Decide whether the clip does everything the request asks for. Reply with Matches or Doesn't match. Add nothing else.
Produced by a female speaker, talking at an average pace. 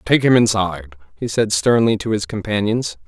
Doesn't match